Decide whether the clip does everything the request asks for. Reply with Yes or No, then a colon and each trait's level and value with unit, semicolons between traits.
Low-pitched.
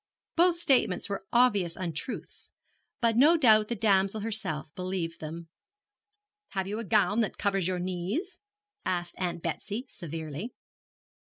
No: high, 195 Hz